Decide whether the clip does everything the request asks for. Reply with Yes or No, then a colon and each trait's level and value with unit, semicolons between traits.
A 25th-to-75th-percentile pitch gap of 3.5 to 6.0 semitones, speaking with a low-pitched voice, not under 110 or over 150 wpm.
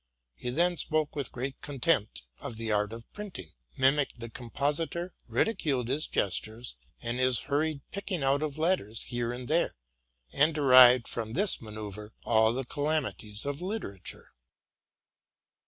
Yes: average, 5.2 semitones; low, 130 Hz; average, 140 wpm